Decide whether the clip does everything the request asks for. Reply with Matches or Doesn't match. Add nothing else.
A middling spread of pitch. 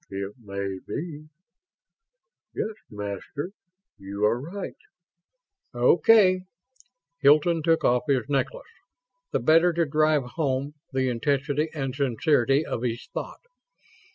Matches